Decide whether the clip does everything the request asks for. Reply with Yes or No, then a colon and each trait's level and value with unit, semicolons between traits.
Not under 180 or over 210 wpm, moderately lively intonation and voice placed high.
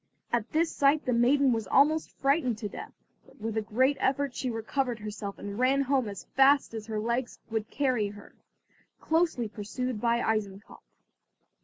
No: average, 170 wpm; average, 4.2 semitones; high, 240 Hz